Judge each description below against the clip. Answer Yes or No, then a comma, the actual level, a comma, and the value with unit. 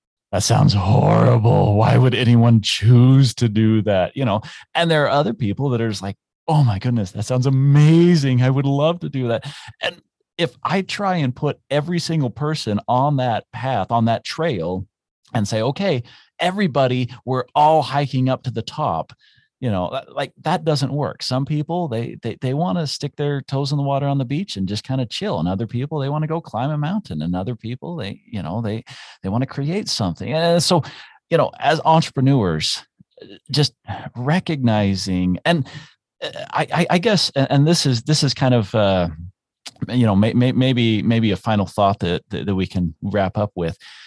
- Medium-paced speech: Yes, average, 195 wpm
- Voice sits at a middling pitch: No, low, 130 Hz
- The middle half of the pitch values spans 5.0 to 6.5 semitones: Yes, wide, 5.4 semitones